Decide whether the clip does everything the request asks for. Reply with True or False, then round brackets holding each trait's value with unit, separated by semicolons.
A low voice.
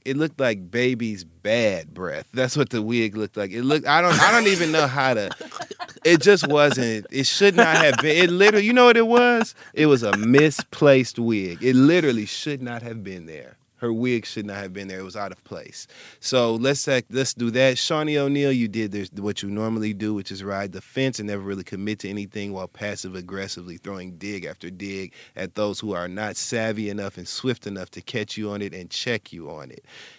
True (110 Hz)